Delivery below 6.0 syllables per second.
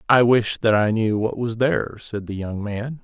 Yes: 4.6 syllables/s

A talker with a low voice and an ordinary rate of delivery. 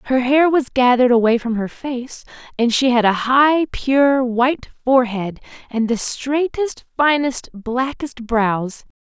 No: very high, 255 Hz; average, 145 wpm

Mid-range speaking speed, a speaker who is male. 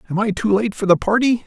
No: fast, 285 wpm; male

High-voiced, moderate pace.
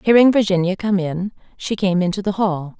Yes: high, 195 Hz; average, 195 wpm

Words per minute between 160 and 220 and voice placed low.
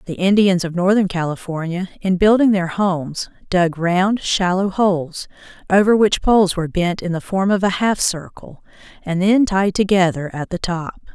No: average, 170 wpm; medium, 185 Hz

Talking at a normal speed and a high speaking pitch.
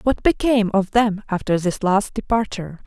Yes: average, 165 wpm; high, 210 Hz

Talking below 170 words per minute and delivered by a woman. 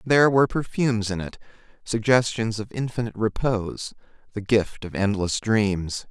No: average, 140 wpm; male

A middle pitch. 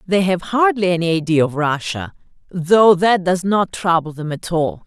Yes: medium, 175 Hz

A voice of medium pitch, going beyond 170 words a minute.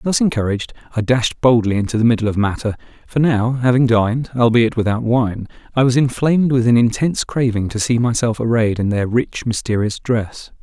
No: low, 120 Hz; average, 185 wpm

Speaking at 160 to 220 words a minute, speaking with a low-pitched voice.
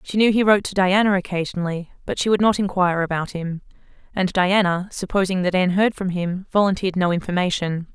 No: average, 190 wpm; medium, 185 Hz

